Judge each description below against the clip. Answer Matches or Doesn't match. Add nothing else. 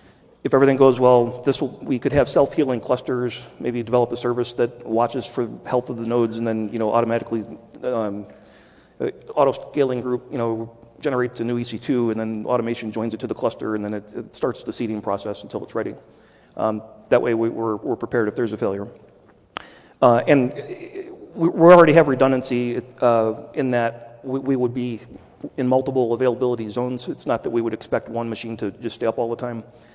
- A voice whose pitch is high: Doesn't match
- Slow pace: Doesn't match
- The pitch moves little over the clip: Matches